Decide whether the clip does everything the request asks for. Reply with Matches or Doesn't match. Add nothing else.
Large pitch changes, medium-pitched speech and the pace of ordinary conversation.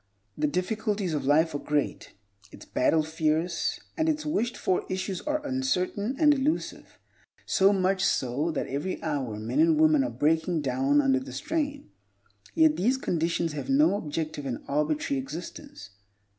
Matches